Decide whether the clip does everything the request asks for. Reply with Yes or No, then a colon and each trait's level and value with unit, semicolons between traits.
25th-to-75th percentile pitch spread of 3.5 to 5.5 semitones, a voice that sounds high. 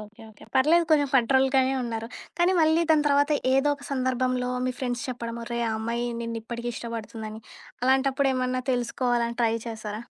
No: narrow, 2.5 semitones; very high, 250 Hz